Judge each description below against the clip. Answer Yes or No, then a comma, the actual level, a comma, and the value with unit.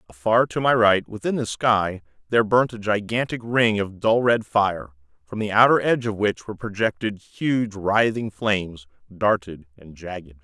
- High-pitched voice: No, low, 105 Hz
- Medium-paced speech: Yes, average, 170 wpm